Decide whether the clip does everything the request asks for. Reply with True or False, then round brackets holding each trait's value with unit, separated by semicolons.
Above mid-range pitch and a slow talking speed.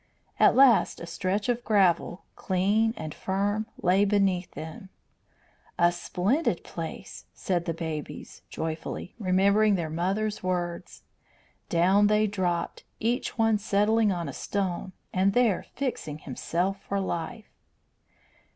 True (195 Hz; 125 wpm)